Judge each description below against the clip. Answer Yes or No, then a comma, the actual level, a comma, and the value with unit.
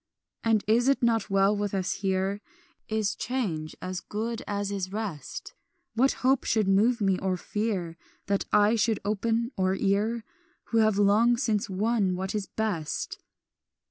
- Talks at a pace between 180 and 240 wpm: No, average, 155 wpm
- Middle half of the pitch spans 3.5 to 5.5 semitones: No, average, 2.7 semitones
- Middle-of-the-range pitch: No, high, 205 Hz